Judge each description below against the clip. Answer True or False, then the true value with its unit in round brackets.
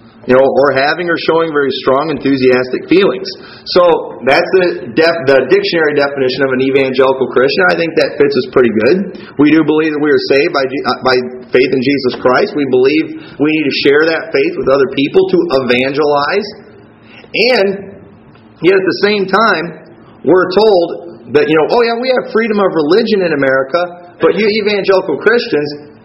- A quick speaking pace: False (180 wpm)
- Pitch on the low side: False (165 Hz)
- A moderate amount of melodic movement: False (8.3 semitones)